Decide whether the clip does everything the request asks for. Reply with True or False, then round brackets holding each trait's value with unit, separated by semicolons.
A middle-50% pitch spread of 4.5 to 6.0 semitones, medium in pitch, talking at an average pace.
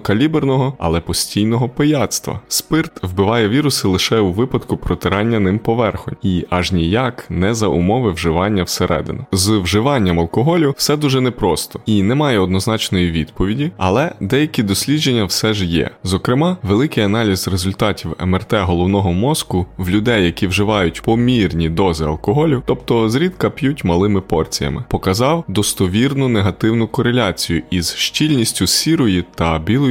False (5.2 semitones; 105 Hz; 130 wpm)